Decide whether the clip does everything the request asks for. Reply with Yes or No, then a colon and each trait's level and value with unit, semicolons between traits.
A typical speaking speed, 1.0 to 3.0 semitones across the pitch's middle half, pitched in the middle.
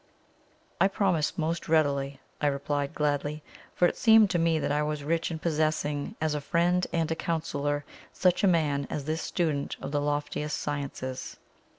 Yes: average, 170 wpm; narrow, 2.6 semitones; medium, 150 Hz